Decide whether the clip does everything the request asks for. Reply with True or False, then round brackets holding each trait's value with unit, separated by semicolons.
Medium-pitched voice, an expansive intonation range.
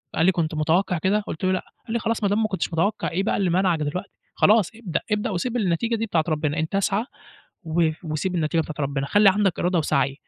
False (180 Hz; 4.4 semitones)